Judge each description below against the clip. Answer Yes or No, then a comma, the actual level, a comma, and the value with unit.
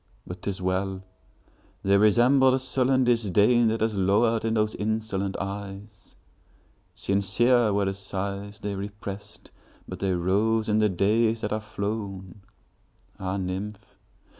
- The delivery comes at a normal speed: No, slow, 115 wpm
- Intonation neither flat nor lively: No, narrow, 2.3 semitones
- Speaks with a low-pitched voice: Yes, low, 105 Hz